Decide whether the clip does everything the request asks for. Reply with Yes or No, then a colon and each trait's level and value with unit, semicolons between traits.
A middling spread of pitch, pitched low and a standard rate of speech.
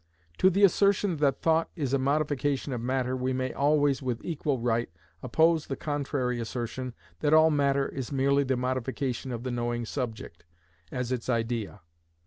Yes: average, 3.0 semitones; low, 130 Hz; average, 165 wpm